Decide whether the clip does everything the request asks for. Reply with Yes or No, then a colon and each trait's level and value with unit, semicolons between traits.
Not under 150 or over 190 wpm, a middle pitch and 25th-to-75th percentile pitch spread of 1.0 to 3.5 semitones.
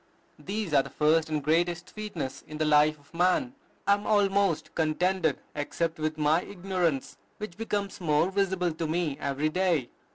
No: average, 165 wpm; medium, 170 Hz; average, 3.9 semitones